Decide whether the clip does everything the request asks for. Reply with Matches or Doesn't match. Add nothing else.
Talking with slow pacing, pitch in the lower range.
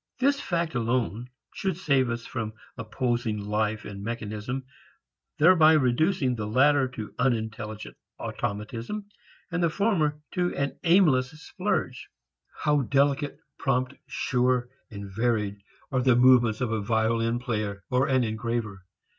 Matches